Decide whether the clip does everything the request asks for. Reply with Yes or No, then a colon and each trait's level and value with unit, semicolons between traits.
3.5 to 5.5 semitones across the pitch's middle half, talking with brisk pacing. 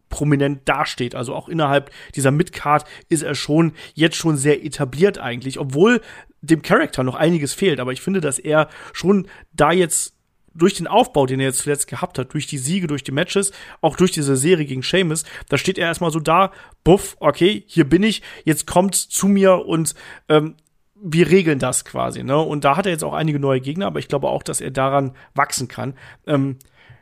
Yes: average, 4.2 semitones; fast, 200 wpm